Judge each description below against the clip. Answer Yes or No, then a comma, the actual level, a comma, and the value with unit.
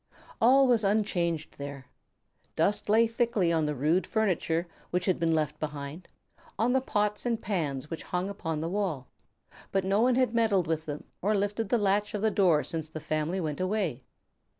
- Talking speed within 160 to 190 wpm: Yes, average, 185 wpm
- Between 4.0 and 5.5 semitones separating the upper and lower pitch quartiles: Yes, average, 5.1 semitones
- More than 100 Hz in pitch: Yes, medium, 185 Hz